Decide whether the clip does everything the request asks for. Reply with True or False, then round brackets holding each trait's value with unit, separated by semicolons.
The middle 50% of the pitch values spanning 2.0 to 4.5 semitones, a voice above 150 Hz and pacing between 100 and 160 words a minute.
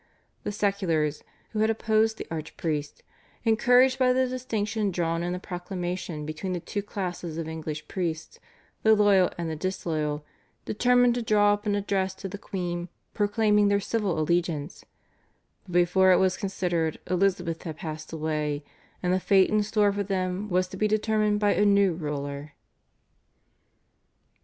True (3.9 semitones; 185 Hz; 155 wpm)